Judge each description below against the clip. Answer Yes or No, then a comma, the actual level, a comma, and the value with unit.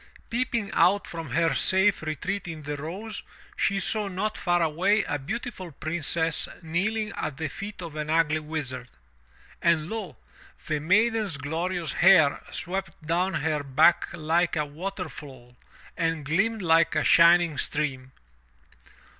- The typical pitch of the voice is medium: Yes, medium, 165 Hz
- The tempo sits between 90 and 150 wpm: Yes, average, 140 wpm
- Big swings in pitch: No, average, 4.1 semitones